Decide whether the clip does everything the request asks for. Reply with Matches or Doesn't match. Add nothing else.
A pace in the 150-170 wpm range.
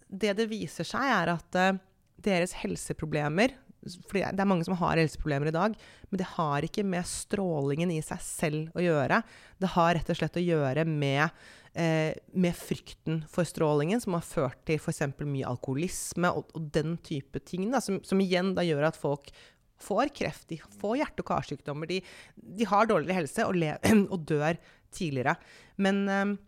Doesn't match